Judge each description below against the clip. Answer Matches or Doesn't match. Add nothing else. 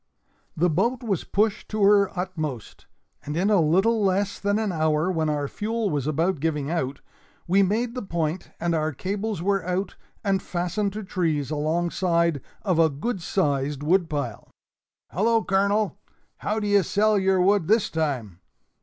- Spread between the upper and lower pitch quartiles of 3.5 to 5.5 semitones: Matches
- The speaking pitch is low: Doesn't match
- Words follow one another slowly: Doesn't match